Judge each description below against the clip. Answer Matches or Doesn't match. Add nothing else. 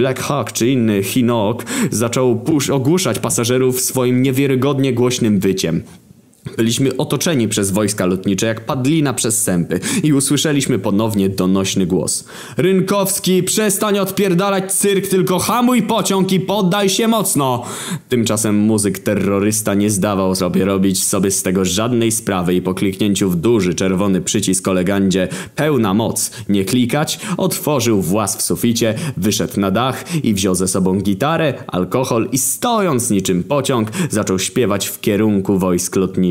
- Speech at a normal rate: Matches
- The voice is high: Doesn't match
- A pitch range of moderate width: Doesn't match